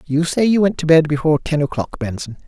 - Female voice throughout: No, male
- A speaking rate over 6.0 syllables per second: Yes, 6.2 syllables/s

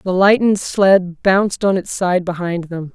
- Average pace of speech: Yes, average, 185 wpm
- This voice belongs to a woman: Yes, female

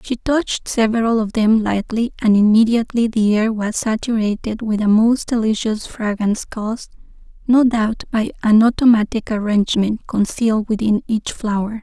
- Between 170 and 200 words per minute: No, average, 140 wpm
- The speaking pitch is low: No, high, 220 Hz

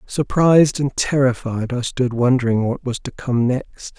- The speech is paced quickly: No, average, 165 wpm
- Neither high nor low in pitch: No, low, 130 Hz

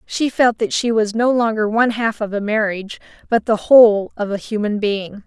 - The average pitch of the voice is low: No, high, 220 Hz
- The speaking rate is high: Yes, fast, 215 wpm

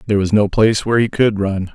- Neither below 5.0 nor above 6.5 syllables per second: No, 6.9 syllables/s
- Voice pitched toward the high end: No, low, 105 Hz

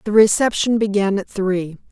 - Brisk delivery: No, average, 155 wpm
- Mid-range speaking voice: No, high, 205 Hz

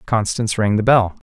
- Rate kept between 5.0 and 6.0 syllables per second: Yes, 5.7 syllables/s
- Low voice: Yes, low, 105 Hz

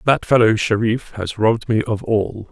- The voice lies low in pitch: Yes, low, 110 Hz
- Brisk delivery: No, average, 190 wpm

